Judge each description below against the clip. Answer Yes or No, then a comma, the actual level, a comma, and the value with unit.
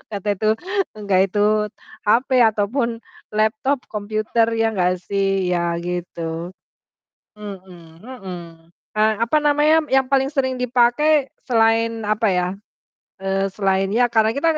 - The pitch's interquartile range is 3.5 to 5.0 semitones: Yes, average, 4.0 semitones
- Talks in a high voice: Yes, high, 215 Hz